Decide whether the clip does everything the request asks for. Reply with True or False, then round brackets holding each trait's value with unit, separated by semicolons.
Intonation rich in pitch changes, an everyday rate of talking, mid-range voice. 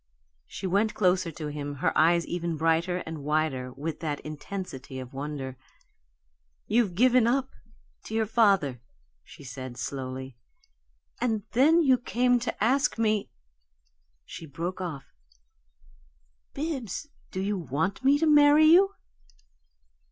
False (8.6 semitones; 130 wpm; 180 Hz)